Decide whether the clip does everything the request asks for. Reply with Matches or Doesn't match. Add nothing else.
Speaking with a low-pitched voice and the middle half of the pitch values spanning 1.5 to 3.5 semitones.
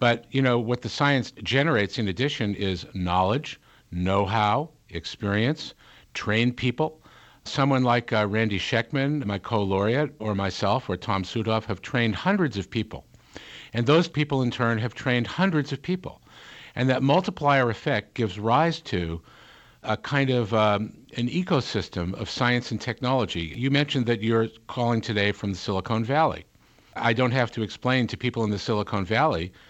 Doesn't match